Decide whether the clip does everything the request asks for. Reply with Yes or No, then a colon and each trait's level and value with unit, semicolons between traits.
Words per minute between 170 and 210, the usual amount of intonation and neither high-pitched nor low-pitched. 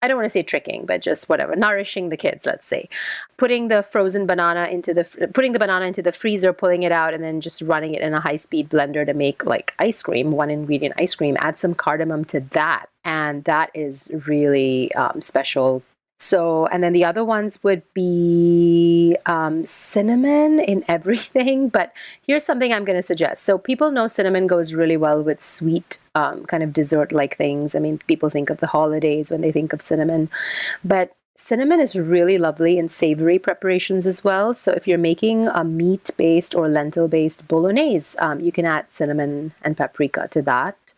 Yes: average, 200 wpm; average, 3.8 semitones; medium, 170 Hz